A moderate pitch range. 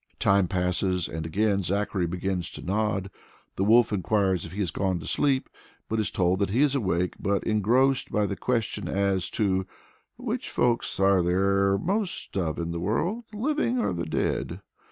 Yes: average, 3.4 semitones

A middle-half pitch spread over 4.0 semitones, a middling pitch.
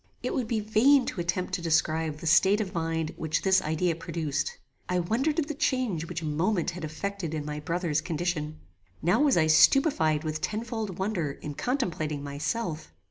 Yes: average, 5.3 semitones; medium, 170 Hz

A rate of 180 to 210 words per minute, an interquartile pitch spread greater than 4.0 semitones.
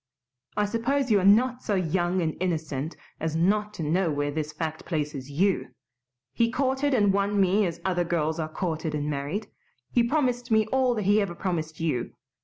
Yes: average, 190 wpm; average, 5.2 semitones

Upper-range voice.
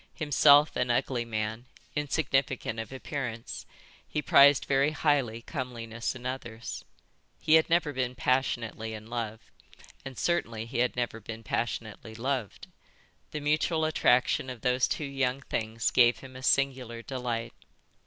No: low, 125 Hz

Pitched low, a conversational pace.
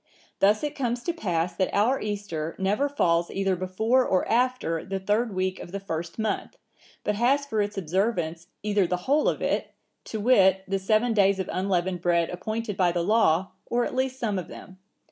No: high, 195 Hz; average, 195 wpm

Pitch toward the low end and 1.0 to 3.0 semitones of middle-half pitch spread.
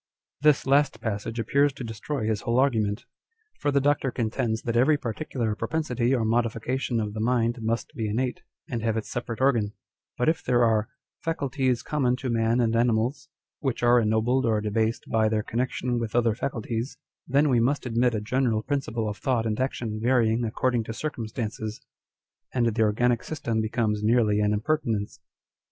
Yes: low, 115 Hz; narrow, 2.6 semitones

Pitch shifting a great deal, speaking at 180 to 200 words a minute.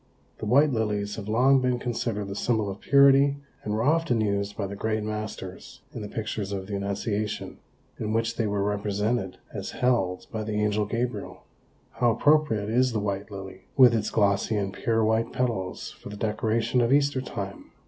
No: average, 2.9 semitones; average, 185 wpm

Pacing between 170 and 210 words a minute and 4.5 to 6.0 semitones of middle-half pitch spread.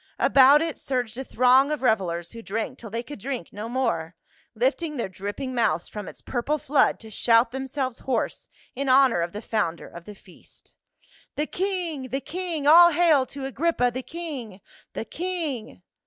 Yes: average, 185 wpm; average, 4.9 semitones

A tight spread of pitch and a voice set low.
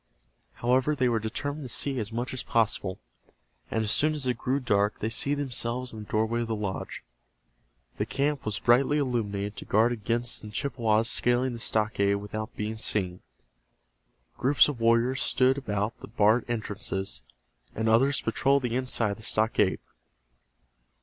No: average, 3.2 semitones; low, 115 Hz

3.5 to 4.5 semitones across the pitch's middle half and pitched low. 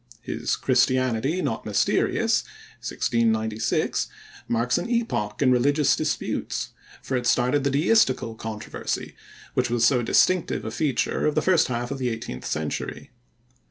Yes: average, 3.9 semitones; low, 125 Hz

